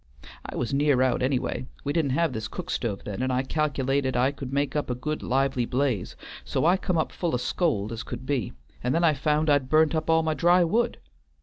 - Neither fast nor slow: No, fast, 235 wpm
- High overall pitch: No, medium, 140 Hz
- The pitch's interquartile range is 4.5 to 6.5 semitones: No, average, 3.8 semitones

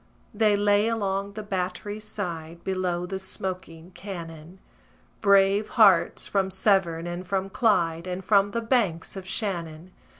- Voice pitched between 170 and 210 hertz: Yes, high, 190 Hz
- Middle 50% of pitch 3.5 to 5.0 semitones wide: No, average, 2.8 semitones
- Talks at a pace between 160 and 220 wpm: No, slow, 135 wpm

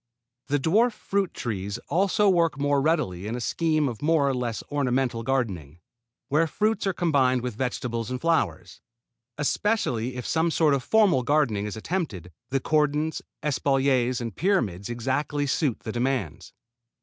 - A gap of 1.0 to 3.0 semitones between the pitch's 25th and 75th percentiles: No, average, 5.2 semitones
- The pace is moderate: Yes, average, 150 wpm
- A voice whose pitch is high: No, low, 135 Hz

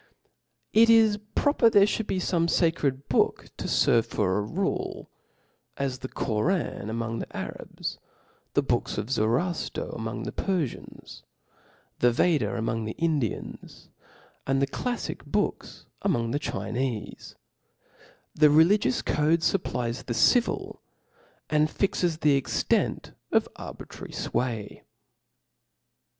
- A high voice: No, medium, 140 Hz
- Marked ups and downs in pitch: Yes, wide, 7.3 semitones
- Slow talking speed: Yes, slow, 120 wpm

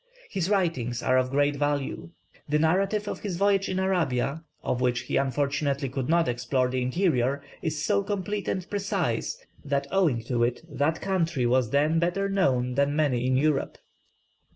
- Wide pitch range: Yes, wide, 6.3 semitones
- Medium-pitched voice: Yes, medium, 145 Hz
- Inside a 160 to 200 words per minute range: Yes, average, 170 wpm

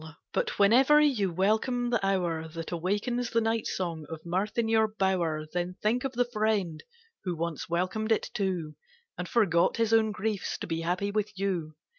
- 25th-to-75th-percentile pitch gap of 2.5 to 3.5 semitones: No, average, 4.4 semitones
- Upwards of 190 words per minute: Yes, average, 200 wpm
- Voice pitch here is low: No, high, 195 Hz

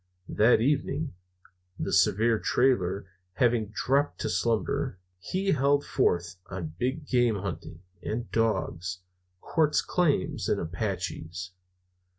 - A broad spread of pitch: Yes, wide, 6.6 semitones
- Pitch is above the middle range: No, low, 115 Hz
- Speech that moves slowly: Yes, slow, 110 wpm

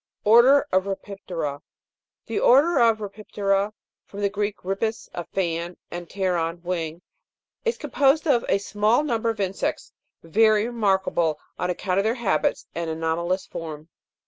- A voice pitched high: Yes, high, 195 Hz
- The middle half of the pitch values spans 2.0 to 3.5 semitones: No, average, 4.3 semitones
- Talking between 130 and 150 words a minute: Yes, average, 145 wpm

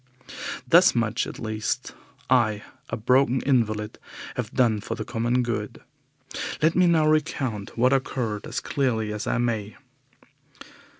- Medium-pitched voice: No, low, 120 Hz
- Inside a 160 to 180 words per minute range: No, slow, 135 wpm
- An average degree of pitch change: Yes, average, 3.5 semitones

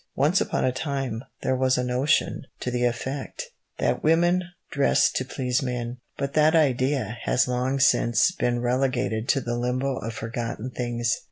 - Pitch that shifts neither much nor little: No, narrow, 2.2 semitones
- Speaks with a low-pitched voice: Yes, low, 130 Hz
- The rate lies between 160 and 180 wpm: Yes, average, 165 wpm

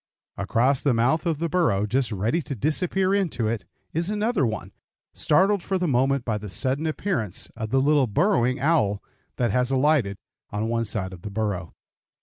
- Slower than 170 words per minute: No, average, 180 wpm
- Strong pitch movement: Yes, wide, 6.7 semitones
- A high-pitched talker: No, low, 130 Hz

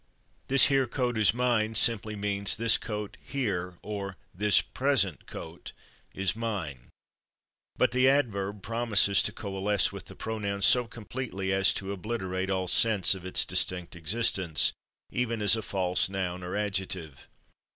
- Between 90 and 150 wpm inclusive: Yes, average, 145 wpm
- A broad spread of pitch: No, average, 3.4 semitones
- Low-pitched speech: Yes, low, 100 Hz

